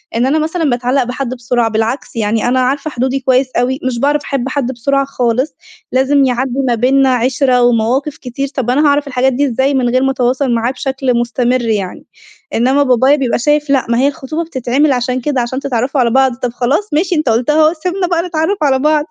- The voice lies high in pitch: Yes, very high, 260 Hz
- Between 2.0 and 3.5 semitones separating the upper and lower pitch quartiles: Yes, narrow, 2.6 semitones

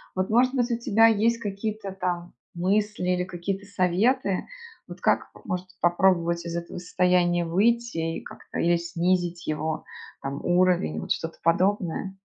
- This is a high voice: No, medium, 180 Hz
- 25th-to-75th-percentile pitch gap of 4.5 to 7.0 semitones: No, average, 2.9 semitones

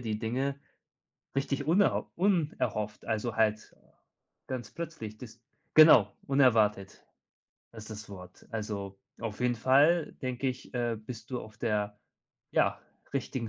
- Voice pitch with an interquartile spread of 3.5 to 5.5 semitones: Yes, average, 4.1 semitones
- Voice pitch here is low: Yes, low, 115 Hz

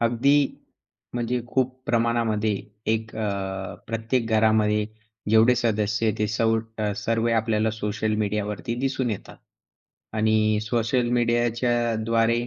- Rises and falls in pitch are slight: Yes, narrow, 1.7 semitones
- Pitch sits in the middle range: No, low, 115 Hz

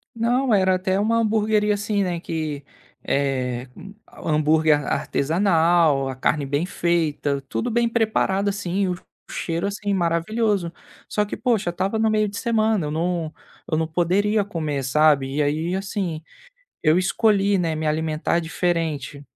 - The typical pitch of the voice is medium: Yes, medium, 175 Hz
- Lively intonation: No, average, 4.8 semitones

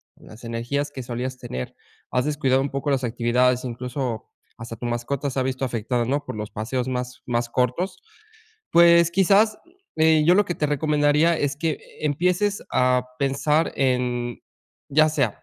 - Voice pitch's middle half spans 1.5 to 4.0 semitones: Yes, average, 3.6 semitones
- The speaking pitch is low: Yes, low, 130 Hz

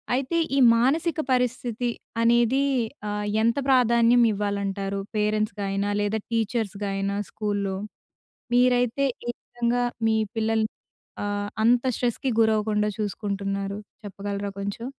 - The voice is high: Yes, high, 220 Hz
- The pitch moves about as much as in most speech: Yes, average, 3.0 semitones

